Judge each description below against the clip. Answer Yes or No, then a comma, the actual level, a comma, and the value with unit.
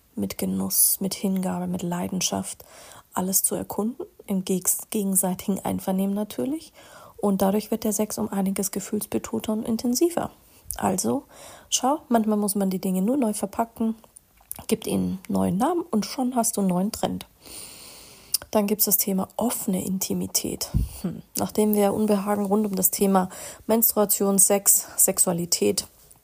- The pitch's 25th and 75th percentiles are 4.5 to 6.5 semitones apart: No, average, 2.8 semitones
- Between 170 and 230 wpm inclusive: No, average, 140 wpm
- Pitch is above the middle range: Yes, high, 205 Hz